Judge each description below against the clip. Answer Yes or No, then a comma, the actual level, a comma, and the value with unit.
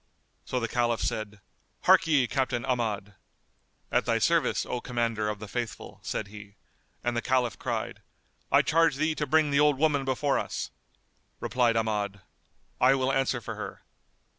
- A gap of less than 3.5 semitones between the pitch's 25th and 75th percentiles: No, average, 3.8 semitones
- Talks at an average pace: Yes, average, 160 wpm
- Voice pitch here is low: Yes, low, 120 Hz